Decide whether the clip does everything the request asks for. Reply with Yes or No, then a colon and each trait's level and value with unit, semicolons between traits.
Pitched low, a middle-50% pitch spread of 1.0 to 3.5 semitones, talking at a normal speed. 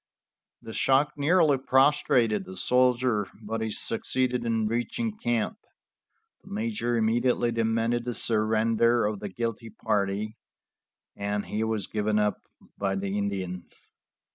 No: low, 115 Hz; average, 2.9 semitones; slow, 125 wpm